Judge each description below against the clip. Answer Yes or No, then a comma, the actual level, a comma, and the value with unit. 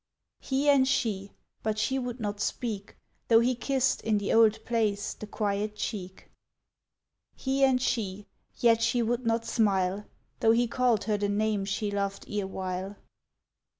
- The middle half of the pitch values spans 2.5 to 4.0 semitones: Yes, average, 2.9 semitones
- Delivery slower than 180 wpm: Yes, average, 155 wpm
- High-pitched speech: Yes, high, 220 Hz